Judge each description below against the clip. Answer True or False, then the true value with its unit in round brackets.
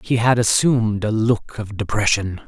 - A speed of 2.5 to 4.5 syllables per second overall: False (4.7 syllables/s)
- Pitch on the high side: False (110 Hz)